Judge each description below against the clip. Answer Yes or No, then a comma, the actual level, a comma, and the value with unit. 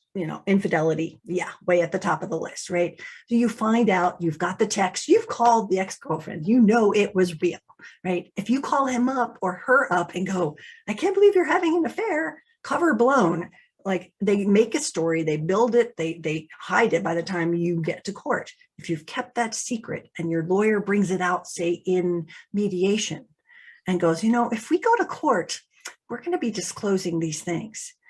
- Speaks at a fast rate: Yes, fast, 210 wpm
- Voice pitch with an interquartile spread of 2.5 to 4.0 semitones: No, wide, 5.5 semitones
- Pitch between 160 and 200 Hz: Yes, high, 190 Hz